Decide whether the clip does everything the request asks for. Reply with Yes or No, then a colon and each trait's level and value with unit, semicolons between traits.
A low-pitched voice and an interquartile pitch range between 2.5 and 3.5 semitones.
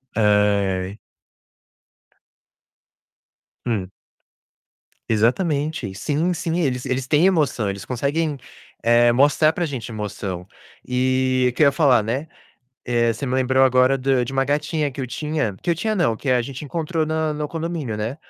No: low, 130 Hz; average, 4.6 semitones